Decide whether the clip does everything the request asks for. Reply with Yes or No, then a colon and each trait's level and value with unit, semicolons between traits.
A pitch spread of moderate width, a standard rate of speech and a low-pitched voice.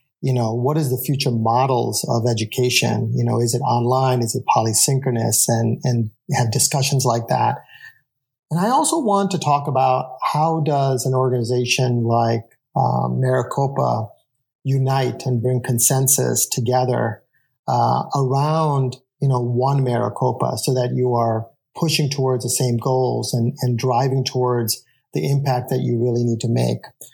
No: narrow, 2.0 semitones; average, 155 wpm; low, 125 Hz